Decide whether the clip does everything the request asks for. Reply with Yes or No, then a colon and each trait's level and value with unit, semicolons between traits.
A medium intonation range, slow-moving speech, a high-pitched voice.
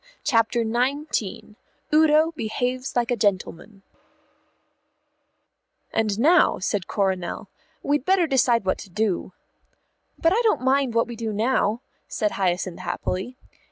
Yes: average, 5.0 semitones; slow, 120 wpm; high, 230 Hz